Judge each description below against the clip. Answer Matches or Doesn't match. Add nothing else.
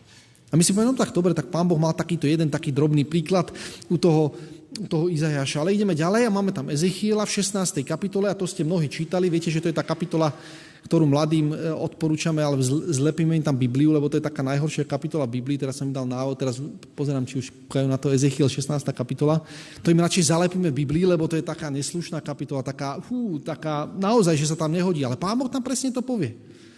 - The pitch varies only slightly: Doesn't match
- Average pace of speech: Doesn't match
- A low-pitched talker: Doesn't match